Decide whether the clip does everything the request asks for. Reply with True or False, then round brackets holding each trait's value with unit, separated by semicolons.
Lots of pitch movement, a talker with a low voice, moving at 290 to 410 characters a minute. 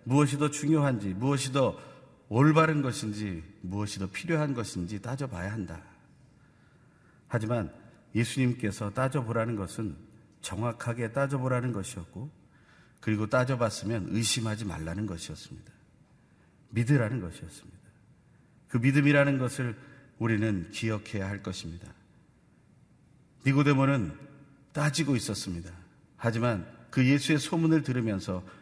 False (5.0 semitones; 120 Hz; 295 characters per minute)